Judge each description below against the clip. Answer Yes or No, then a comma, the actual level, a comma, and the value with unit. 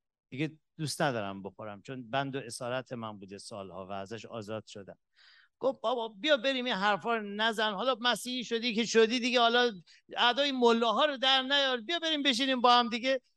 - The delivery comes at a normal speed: No, fast, 185 wpm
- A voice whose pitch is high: Yes, high, 225 Hz